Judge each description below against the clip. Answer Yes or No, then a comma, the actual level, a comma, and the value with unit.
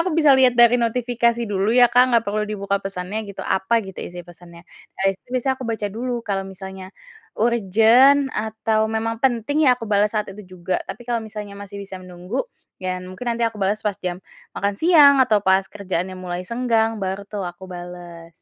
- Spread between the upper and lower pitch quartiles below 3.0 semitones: No, average, 3.7 semitones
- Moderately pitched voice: No, high, 210 Hz